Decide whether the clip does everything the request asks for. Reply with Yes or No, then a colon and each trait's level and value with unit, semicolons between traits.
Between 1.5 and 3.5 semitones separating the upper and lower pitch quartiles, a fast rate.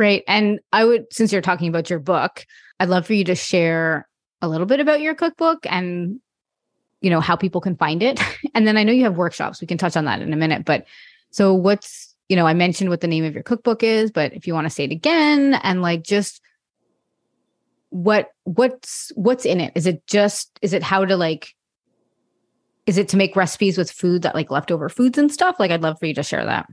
No: average, 4.2 semitones; fast, 235 wpm